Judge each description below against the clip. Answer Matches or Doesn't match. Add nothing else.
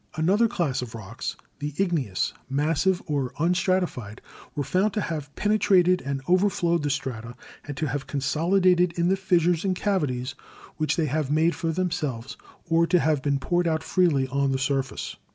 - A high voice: Doesn't match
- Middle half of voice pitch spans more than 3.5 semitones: Matches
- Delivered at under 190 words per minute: Matches